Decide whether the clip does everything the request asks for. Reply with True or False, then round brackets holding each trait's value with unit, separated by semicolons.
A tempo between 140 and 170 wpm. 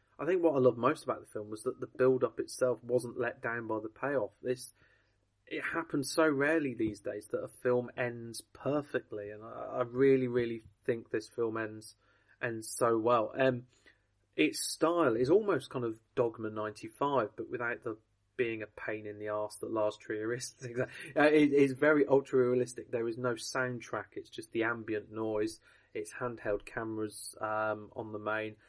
False (180 wpm)